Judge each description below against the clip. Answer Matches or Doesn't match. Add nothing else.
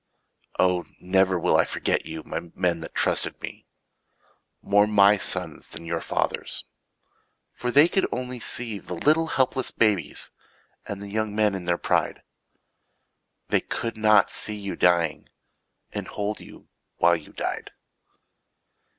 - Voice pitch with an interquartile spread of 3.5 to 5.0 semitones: Matches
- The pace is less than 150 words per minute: Matches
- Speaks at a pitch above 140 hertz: Doesn't match